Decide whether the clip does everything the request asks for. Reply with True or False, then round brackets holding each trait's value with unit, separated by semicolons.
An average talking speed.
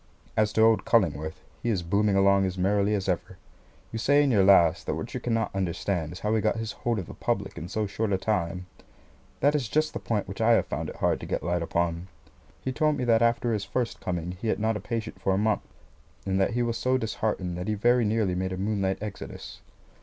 False (245 wpm)